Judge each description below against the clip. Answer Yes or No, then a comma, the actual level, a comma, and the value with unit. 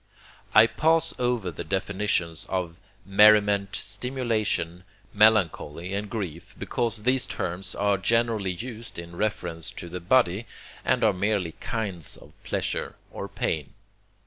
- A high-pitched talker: No, low, 100 Hz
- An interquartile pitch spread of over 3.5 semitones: Yes, average, 3.9 semitones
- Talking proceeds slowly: Yes, slow, 125 wpm